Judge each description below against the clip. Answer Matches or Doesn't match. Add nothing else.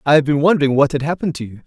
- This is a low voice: Doesn't match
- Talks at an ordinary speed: Doesn't match